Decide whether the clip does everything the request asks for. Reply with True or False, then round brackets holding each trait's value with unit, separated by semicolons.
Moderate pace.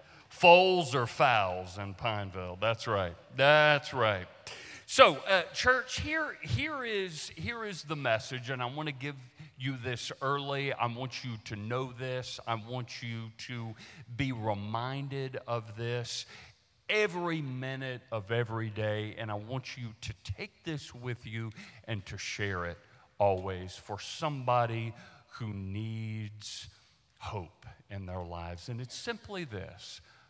True (145 wpm)